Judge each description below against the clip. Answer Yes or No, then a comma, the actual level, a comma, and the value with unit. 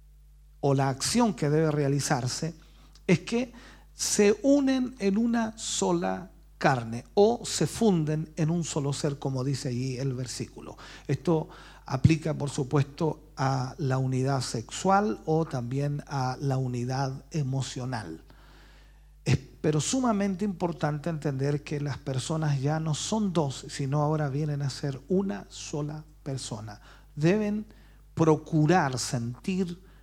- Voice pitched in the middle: Yes, medium, 150 Hz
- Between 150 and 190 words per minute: No, slow, 125 wpm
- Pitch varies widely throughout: No, average, 4.4 semitones